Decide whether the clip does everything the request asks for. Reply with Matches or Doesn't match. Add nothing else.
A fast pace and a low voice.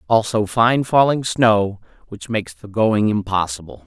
Doesn't match